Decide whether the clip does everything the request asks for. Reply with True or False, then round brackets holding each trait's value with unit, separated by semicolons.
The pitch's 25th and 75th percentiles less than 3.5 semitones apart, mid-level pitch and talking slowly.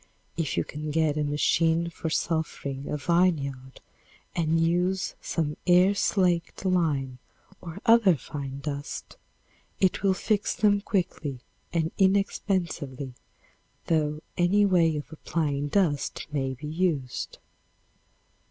False (3.9 semitones; 160 Hz; 115 wpm)